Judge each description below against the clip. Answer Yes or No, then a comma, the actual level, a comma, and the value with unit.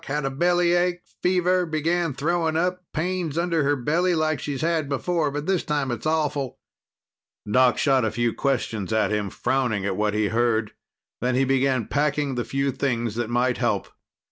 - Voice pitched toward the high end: No, medium, 140 Hz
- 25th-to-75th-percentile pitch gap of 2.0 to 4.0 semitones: No, average, 5.3 semitones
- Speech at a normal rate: Yes, average, 175 wpm